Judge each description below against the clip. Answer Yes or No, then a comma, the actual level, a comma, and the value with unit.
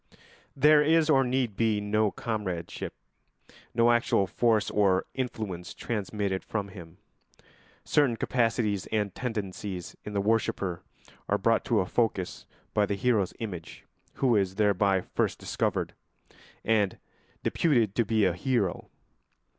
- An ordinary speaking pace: No, slow, 130 wpm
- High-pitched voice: No, low, 105 Hz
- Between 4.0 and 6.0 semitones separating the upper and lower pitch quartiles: No, average, 3.4 semitones